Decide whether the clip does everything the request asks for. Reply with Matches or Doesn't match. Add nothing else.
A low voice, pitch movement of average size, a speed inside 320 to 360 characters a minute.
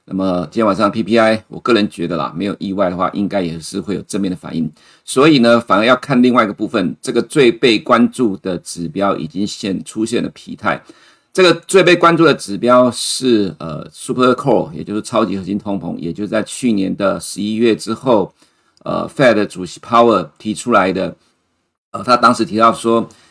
Matches